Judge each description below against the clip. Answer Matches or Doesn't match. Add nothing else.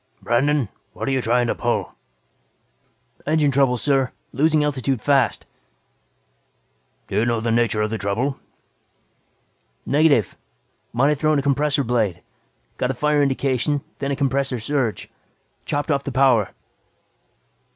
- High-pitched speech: Doesn't match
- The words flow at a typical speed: Doesn't match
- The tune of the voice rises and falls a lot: Doesn't match